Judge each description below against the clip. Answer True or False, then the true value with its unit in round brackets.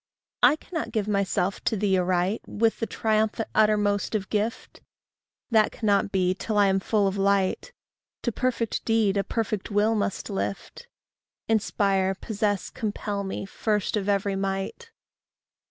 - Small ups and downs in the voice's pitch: True (2.1 semitones)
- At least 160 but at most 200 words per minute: False (145 wpm)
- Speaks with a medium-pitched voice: False (205 Hz)